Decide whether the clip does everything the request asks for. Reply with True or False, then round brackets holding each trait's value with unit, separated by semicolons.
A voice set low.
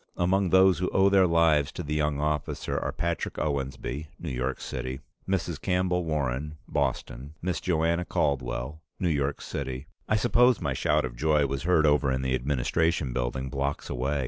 True (75 Hz)